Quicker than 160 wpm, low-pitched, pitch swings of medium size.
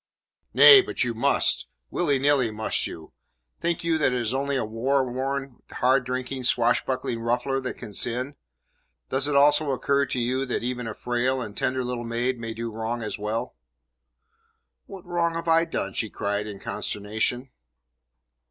Yes: average, 170 wpm; low, 125 Hz; average, 3.1 semitones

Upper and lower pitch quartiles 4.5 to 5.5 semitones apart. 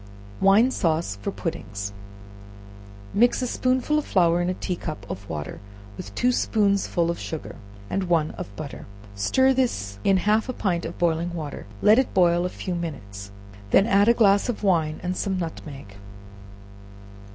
Yes: average, 5.1 semitones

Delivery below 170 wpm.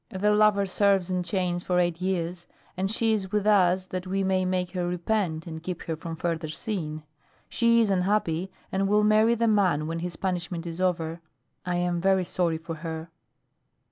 No: average, 190 wpm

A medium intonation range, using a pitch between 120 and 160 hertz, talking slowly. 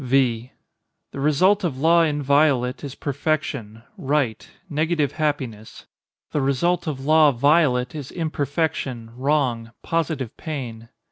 Yes: average, 3.7 semitones; medium, 140 Hz; slow, 105 wpm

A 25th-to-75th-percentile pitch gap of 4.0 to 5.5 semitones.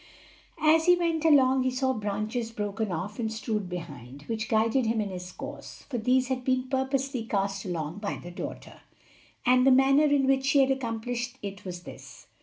Yes: average, 4.6 semitones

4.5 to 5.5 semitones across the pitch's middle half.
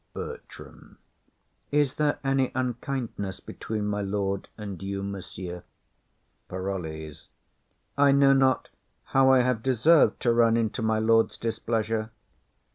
Yes: average, 4.9 semitones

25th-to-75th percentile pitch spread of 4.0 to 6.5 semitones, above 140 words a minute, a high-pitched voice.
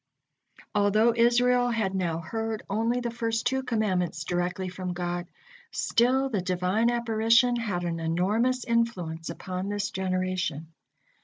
No: average, 4.5 semitones; slow, 135 wpm; high, 205 Hz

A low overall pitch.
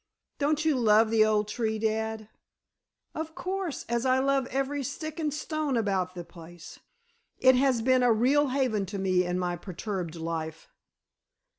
No: high, 225 Hz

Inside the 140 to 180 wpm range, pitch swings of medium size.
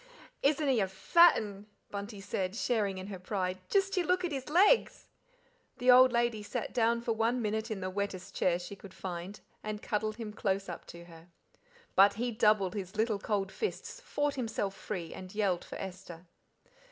No: average, 190 wpm; average, 3.9 semitones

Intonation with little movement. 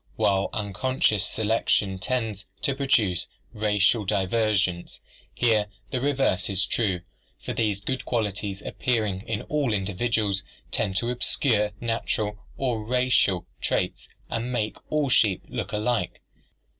No: average, 3.4 semitones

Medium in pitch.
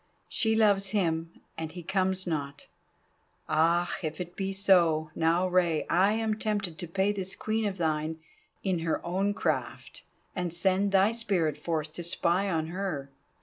Yes: medium, 180 Hz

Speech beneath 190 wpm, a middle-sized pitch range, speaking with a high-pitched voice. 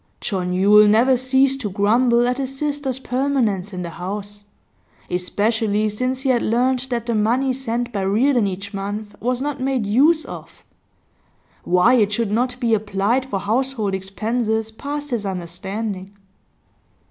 Yes: average, 150 wpm; average, 4.1 semitones; high, 225 Hz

